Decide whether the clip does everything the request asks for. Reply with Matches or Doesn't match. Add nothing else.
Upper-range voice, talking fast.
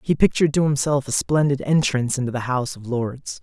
Doesn't match